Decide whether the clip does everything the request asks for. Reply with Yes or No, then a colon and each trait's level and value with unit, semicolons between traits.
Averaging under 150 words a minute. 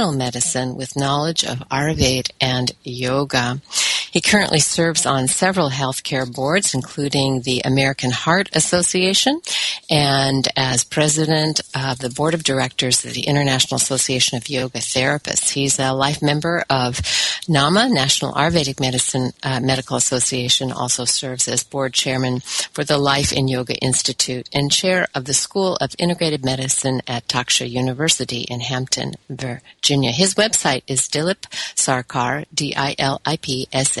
Yes: slow, 135 wpm